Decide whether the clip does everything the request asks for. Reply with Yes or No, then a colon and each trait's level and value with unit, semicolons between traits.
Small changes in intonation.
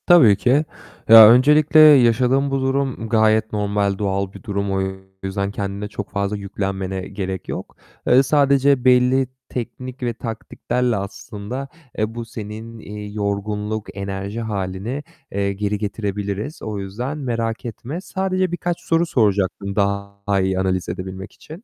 No: average, 4.3 semitones